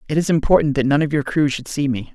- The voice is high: No, medium, 145 Hz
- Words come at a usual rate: No, fast, 310 wpm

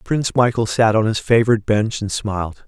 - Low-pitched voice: Yes, low, 110 Hz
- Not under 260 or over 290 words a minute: No, average, 200 wpm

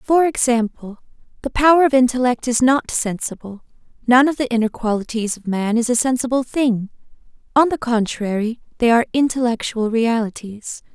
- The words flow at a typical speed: Yes, average, 150 wpm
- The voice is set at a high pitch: Yes, high, 240 Hz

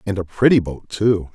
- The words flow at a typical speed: No, fast, 225 wpm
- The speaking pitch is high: No, low, 100 Hz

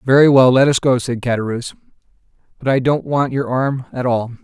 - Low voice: Yes, low, 130 Hz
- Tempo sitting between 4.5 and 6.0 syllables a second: Yes, 5.7 syllables/s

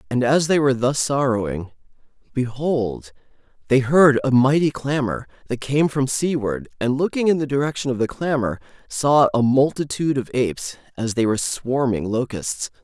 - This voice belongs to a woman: No, male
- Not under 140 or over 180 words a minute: Yes, average, 160 wpm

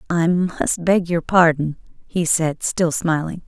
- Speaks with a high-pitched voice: No, medium, 165 Hz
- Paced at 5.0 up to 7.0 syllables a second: No, 3.7 syllables/s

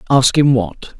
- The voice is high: No, low, 130 Hz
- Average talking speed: Yes, average, 180 wpm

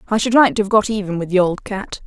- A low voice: No, high, 205 Hz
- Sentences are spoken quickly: Yes, fast, 320 wpm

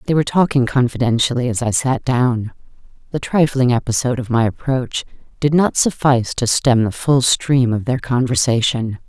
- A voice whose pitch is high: No, low, 125 Hz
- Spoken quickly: No, average, 165 wpm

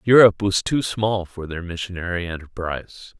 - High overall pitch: No, very low, 95 Hz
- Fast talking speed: No, average, 150 wpm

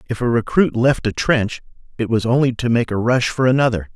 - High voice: No, low, 120 Hz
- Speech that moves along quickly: Yes, fast, 230 wpm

